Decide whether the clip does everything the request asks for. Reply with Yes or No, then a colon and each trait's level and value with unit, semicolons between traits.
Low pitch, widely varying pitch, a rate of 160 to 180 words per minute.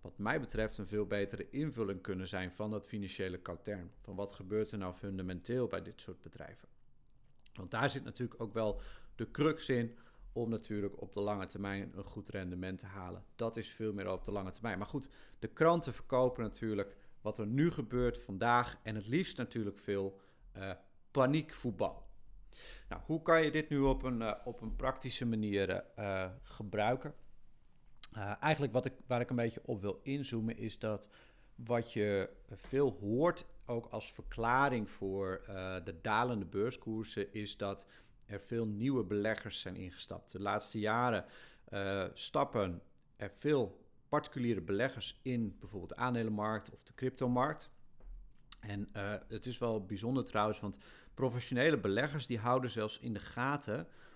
No: low, 110 Hz; average, 3.8 semitones; average, 165 wpm